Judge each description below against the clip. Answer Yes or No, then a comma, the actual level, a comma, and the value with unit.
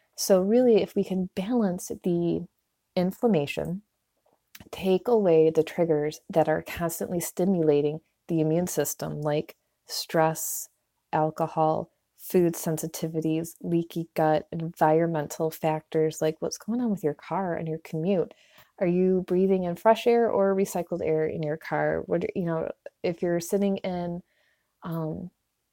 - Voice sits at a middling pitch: Yes, medium, 170 Hz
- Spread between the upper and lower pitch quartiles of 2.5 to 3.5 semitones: Yes, average, 3.1 semitones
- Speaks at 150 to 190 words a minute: No, slow, 135 wpm